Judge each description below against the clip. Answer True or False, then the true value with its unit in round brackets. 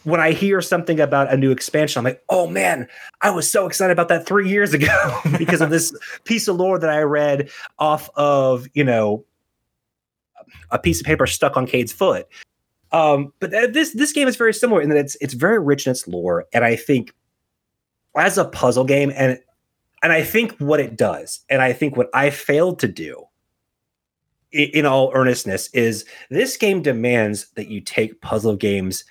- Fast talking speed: False (190 wpm)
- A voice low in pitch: False (145 Hz)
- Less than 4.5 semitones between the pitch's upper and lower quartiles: False (5.2 semitones)